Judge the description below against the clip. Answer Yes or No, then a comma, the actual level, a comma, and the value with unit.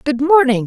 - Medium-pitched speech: No, very high, 275 Hz